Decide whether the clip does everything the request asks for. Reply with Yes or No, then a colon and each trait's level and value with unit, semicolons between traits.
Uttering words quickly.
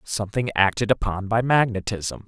No: slow, 130 wpm